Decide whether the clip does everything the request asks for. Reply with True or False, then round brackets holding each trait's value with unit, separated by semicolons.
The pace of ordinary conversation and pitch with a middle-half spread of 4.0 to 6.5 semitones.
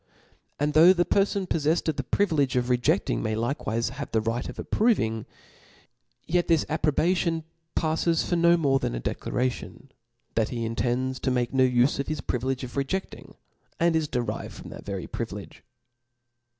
True (170 wpm; 5.1 semitones)